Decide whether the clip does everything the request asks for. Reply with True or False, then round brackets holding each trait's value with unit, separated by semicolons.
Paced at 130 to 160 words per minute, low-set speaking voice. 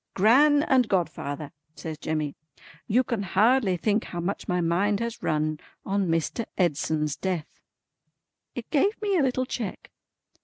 False (145 wpm; 195 Hz)